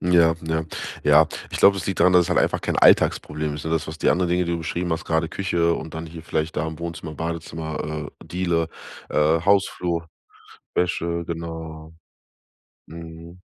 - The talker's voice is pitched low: Yes, very low, 80 Hz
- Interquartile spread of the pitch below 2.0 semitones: Yes, narrow, 1.3 semitones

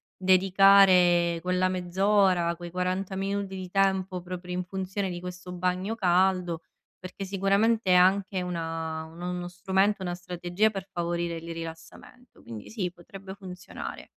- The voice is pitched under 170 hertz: No, medium, 185 Hz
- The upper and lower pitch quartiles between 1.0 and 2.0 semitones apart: Yes, narrow, 1.7 semitones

